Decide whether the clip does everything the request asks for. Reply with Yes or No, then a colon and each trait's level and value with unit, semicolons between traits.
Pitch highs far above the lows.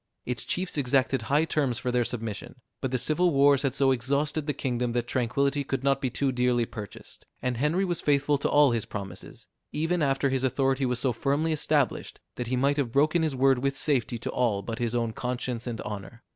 No: average, 2.8 semitones